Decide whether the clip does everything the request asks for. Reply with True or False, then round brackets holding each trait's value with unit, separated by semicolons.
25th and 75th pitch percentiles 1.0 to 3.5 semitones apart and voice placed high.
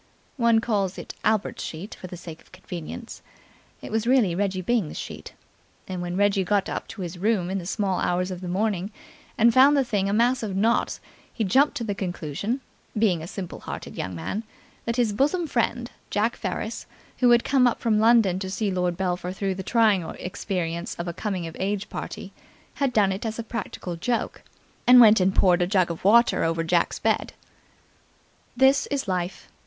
False (4.3 semitones; 200 Hz)